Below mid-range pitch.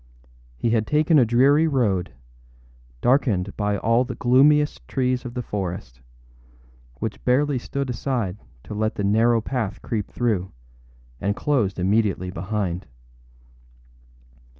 Yes: low, 115 Hz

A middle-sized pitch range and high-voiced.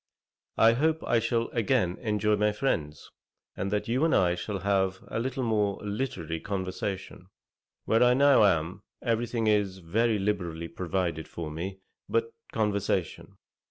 No: average, 3.8 semitones; low, 105 Hz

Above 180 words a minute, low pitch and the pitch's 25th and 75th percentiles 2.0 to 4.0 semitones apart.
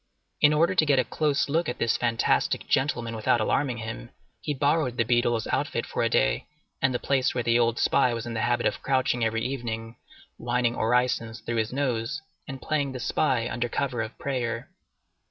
Yes: average, 195 wpm; low, 120 Hz; average, 2.8 semitones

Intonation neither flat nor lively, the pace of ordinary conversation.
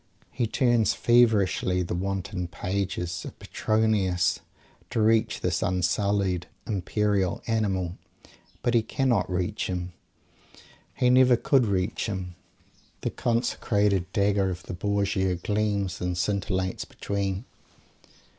No: average, 3.1 semitones; slow, 110 wpm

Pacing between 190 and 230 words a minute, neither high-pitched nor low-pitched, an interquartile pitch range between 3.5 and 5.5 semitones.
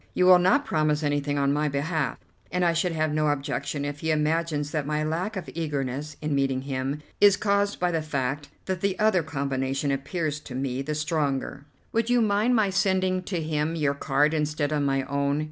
Yes: average, 200 wpm; medium, 150 Hz; average, 3.9 semitones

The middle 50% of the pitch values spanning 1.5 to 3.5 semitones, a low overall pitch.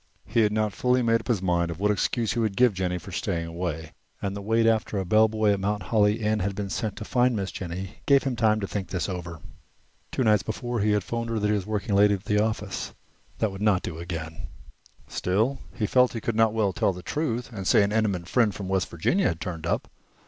Yes: average, 3.2 semitones; low, 105 Hz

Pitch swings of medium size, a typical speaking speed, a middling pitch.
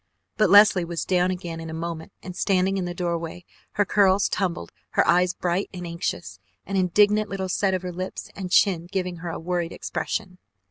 No: narrow, 2.1 semitones; average, 190 wpm; medium, 180 Hz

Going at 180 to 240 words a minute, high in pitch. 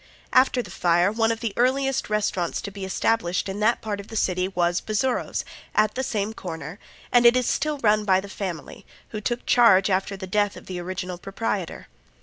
Yes: average, 200 wpm; high, 205 Hz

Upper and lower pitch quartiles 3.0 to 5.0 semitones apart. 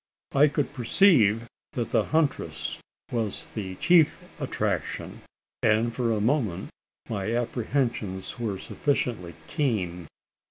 No: wide, 5.4 semitones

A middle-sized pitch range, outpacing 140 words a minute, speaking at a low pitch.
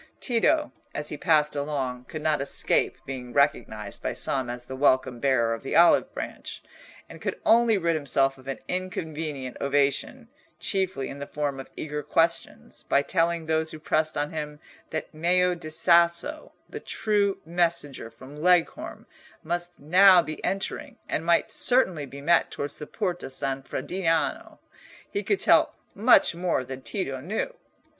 No: average, 4.3 semitones; average, 160 wpm; medium, 155 Hz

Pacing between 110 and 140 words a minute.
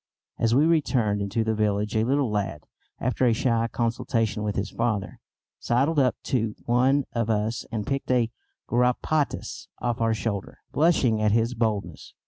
No: average, 160 wpm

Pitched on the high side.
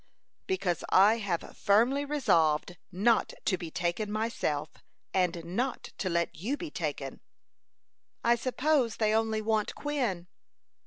Yes: high, 215 Hz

